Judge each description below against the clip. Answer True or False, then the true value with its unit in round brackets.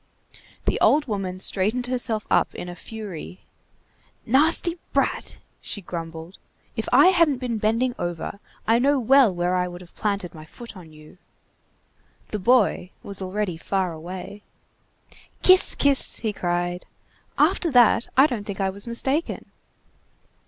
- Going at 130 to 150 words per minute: True (145 wpm)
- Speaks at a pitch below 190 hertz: False (205 Hz)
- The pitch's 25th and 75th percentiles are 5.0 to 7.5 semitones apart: True (5.6 semitones)